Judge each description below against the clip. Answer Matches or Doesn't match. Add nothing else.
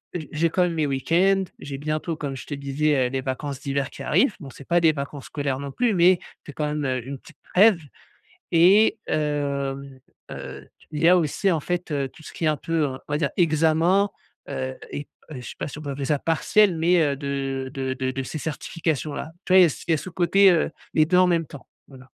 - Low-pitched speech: Doesn't match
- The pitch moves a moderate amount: Matches